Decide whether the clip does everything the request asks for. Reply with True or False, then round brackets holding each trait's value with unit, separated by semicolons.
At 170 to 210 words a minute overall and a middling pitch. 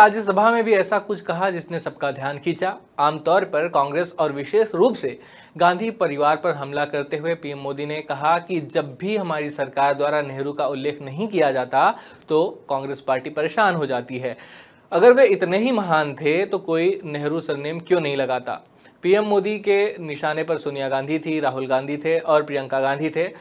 True (190 wpm; 155 Hz)